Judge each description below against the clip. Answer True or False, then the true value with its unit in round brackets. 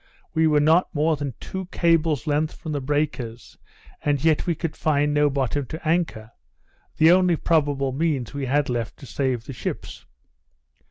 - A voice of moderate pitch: True (150 Hz)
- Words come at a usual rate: True (170 wpm)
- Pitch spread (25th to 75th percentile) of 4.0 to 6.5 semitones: False (2.8 semitones)